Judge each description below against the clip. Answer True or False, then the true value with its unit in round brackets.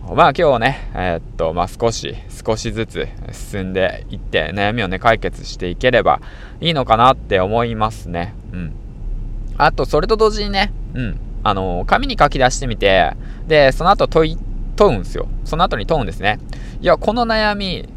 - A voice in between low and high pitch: False (115 Hz)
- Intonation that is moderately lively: True (4.6 semitones)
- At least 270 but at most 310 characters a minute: True (295 characters per minute)